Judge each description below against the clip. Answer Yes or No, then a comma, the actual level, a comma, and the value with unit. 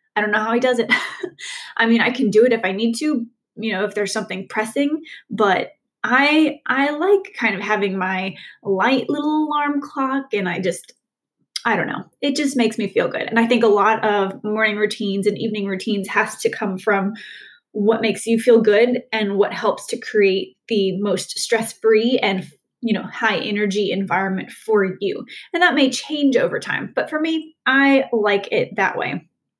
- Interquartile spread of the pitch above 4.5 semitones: Yes, average, 5.1 semitones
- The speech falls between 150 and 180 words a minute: No, average, 195 wpm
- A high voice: Yes, high, 225 Hz